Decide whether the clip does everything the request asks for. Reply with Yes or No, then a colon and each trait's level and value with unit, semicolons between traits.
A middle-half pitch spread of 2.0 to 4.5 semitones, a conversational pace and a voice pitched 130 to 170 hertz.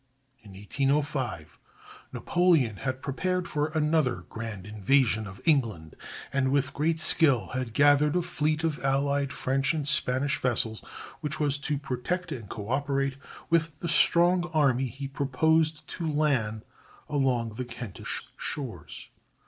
No: average, 3.8 semitones; slow, 130 wpm; medium, 140 Hz